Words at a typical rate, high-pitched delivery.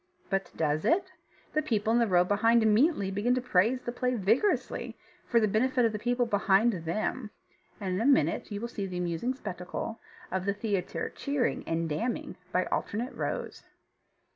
Yes: average, 175 wpm; high, 215 Hz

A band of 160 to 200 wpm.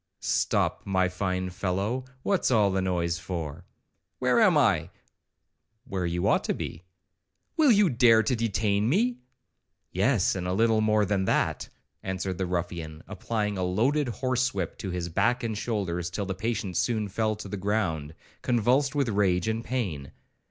Yes: average, 165 wpm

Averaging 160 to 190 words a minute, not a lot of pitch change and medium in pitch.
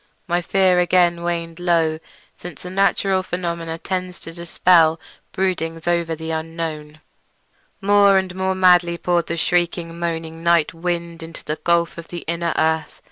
No: average, 150 wpm; narrow, 1.5 semitones; medium, 170 Hz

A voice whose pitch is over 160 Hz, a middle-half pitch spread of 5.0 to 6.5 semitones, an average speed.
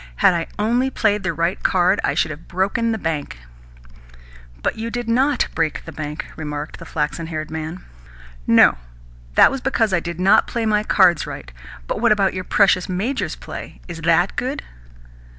Yes: medium, 185 Hz; average, 5.3 semitones; average, 180 wpm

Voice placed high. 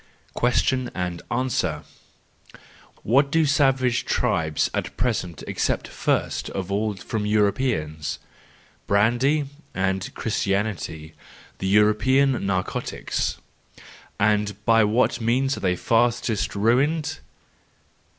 No: low, 110 Hz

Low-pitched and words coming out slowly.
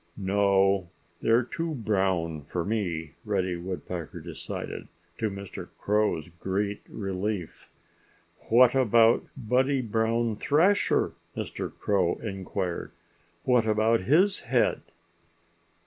Yes: low, 105 Hz; slow, 100 wpm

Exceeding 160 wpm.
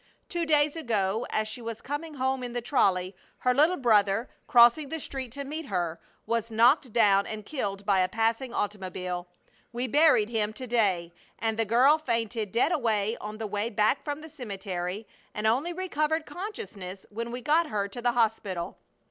Yes: average, 180 wpm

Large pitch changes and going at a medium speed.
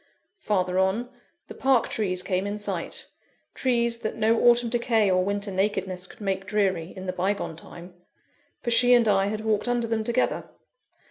No: average, 3.6 semitones; average, 175 wpm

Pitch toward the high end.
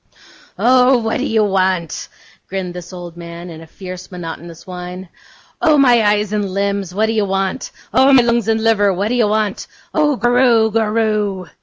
Yes: high, 205 Hz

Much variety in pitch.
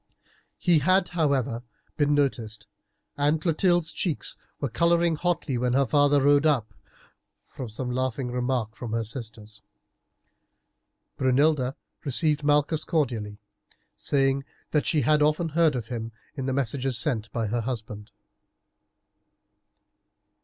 No: average, 4.2 semitones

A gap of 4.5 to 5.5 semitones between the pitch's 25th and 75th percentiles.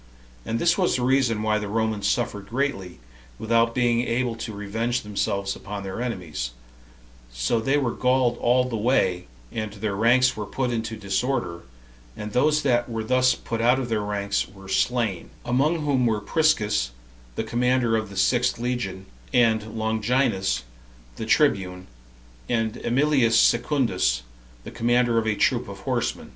No: average, 3.4 semitones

